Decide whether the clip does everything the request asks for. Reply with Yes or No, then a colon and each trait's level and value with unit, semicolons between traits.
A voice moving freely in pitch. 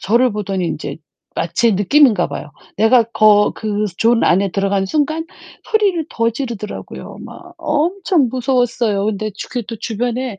No: average, 4.7 semitones